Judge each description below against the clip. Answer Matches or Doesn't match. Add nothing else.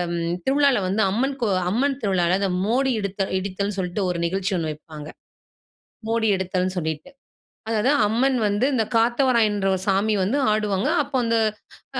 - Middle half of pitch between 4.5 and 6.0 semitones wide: Doesn't match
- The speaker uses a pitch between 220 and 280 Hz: Doesn't match